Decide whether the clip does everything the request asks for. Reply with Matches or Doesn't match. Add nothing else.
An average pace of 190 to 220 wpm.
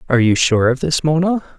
Doesn't match